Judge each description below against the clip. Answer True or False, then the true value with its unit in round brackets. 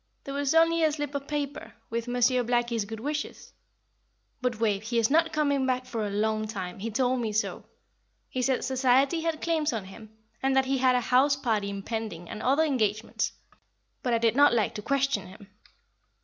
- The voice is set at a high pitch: True (250 Hz)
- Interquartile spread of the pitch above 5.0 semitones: False (4.2 semitones)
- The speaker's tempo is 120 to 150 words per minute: False (195 wpm)